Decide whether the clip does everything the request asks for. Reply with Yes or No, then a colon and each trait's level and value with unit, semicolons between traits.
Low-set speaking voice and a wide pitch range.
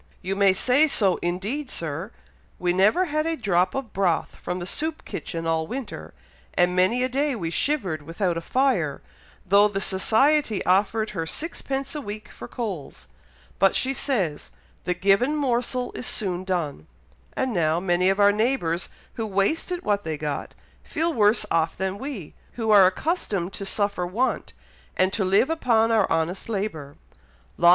No: high, 200 Hz; wide, 6.0 semitones